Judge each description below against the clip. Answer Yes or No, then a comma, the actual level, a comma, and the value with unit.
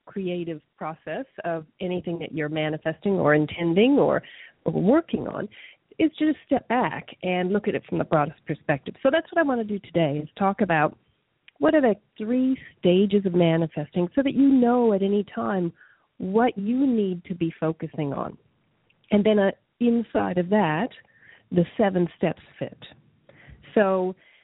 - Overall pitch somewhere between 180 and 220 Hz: Yes, high, 190 Hz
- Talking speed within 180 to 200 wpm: No, average, 165 wpm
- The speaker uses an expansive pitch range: Yes, wide, 5.8 semitones